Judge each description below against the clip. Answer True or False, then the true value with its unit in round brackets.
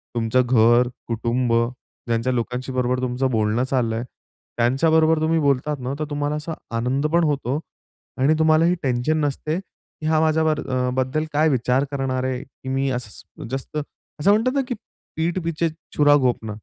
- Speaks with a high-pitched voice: False (135 Hz)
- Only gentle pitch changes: False (3.8 semitones)